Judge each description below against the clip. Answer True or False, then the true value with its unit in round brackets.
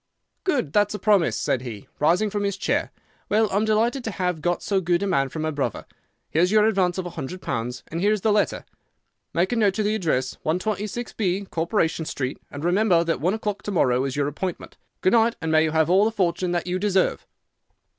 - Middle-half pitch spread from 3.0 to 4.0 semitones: False (4.6 semitones)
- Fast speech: True (220 wpm)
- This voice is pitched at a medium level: True (180 Hz)